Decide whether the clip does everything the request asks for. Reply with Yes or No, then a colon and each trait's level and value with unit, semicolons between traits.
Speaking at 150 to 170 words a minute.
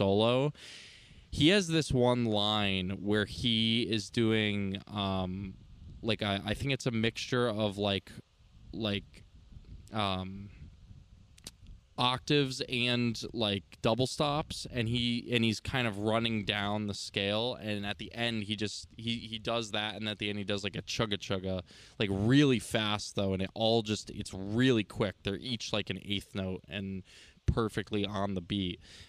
Yes: average, 165 wpm